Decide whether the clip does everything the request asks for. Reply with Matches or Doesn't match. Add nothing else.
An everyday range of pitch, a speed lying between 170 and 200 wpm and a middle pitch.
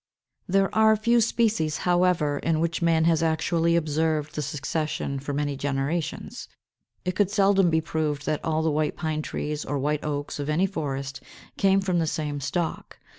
Matches